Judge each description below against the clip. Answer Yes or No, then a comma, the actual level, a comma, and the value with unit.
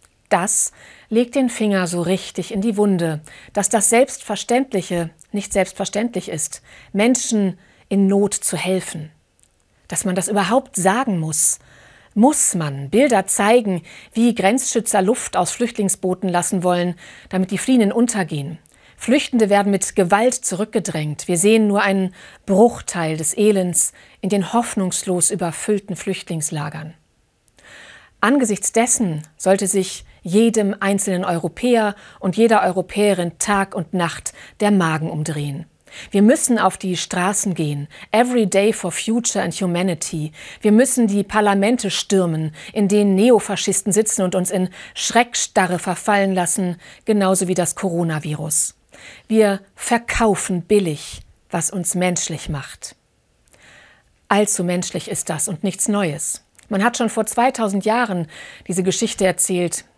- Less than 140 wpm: Yes, average, 130 wpm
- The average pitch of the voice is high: Yes, high, 195 Hz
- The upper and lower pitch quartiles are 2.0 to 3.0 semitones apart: No, average, 3.5 semitones